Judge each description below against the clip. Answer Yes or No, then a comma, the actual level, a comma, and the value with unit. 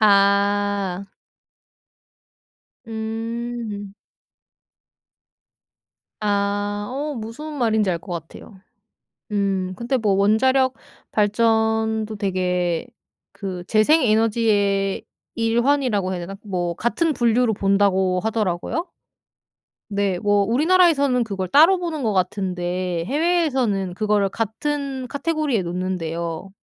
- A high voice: Yes, high, 210 Hz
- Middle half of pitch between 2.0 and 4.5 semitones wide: Yes, average, 3.8 semitones